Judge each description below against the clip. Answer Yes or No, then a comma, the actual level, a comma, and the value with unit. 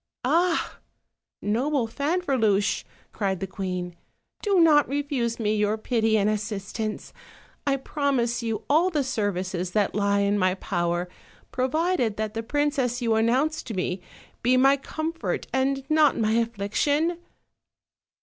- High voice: Yes, high, 235 Hz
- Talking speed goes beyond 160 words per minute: No, slow, 135 wpm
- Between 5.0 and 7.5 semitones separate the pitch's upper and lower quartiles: Yes, wide, 5.6 semitones